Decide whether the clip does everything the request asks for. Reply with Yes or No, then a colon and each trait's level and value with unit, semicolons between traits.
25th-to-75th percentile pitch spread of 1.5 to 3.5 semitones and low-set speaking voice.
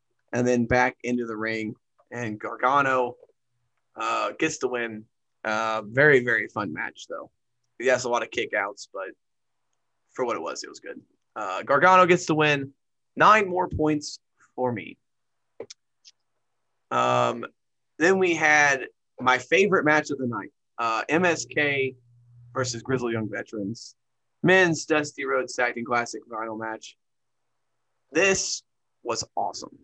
No: average, 4.0 semitones; low, 125 Hz